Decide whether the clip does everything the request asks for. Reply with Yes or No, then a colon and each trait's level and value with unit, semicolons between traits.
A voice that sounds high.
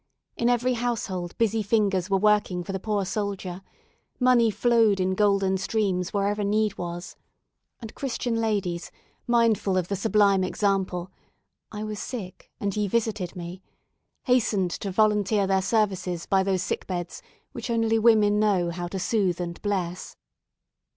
Yes: high, 200 Hz